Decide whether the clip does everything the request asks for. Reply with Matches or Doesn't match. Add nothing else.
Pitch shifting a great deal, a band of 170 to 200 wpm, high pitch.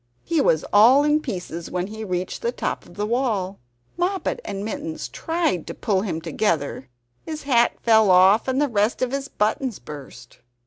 Matches